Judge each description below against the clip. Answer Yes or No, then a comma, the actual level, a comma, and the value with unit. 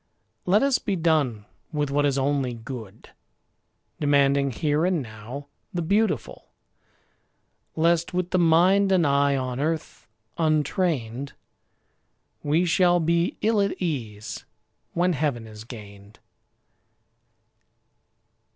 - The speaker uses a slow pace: Yes, slow, 110 wpm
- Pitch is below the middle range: No, medium, 145 Hz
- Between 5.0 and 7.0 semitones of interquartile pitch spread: Yes, average, 5.3 semitones